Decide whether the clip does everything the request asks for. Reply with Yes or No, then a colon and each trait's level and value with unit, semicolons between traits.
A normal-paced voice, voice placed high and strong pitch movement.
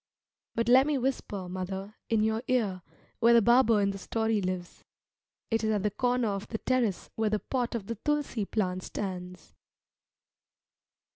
No: average, 165 wpm; high, 220 Hz; average, 3.5 semitones